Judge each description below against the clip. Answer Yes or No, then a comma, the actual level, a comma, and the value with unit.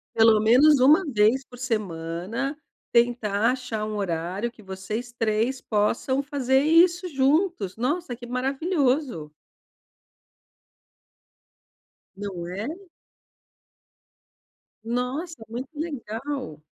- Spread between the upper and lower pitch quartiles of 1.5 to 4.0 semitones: No, average, 4.5 semitones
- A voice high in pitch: Yes, high, 245 Hz